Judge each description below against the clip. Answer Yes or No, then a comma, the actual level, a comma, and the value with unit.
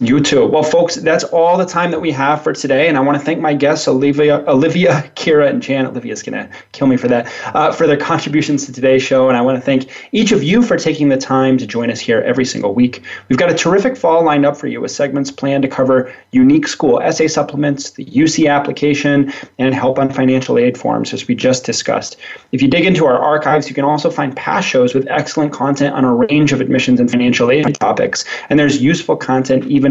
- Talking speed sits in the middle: No, fast, 235 wpm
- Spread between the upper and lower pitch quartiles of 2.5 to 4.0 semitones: Yes, average, 3.2 semitones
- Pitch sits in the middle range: Yes, medium, 145 Hz